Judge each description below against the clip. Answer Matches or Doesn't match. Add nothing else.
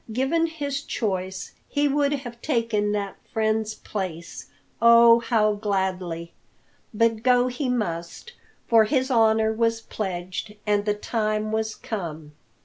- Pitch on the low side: Doesn't match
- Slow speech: Matches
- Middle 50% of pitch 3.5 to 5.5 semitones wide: Doesn't match